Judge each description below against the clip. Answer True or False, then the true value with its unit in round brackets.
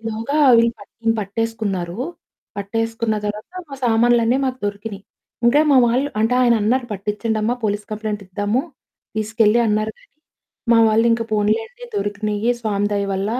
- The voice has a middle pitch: False (220 Hz)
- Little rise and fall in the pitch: True (2.1 semitones)